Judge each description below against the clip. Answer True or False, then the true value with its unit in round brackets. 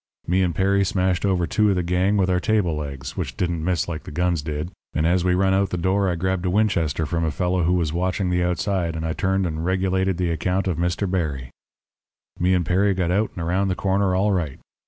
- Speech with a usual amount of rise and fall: False (2.2 semitones)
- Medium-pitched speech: False (90 Hz)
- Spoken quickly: True (240 wpm)